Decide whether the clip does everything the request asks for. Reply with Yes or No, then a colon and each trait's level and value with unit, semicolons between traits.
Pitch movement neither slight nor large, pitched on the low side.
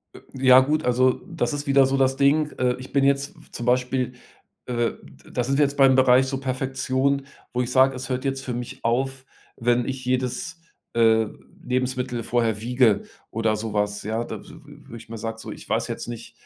No: narrow, 2.1 semitones; low, 130 Hz